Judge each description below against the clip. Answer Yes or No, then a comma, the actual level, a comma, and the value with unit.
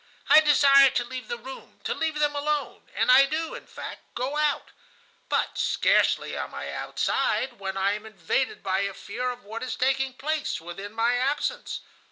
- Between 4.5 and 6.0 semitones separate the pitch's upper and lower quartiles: Yes, average, 4.8 semitones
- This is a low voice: No, very high, 255 Hz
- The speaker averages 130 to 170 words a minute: No, average, 185 wpm